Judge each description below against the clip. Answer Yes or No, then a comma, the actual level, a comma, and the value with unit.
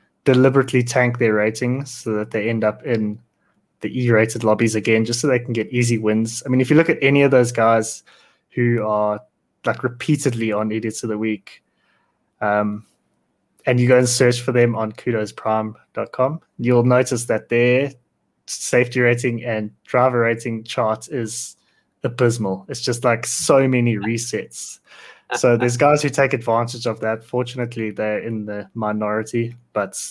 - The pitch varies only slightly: Yes, narrow, 2.3 semitones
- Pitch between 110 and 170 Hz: Yes, low, 120 Hz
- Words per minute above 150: Yes, average, 165 wpm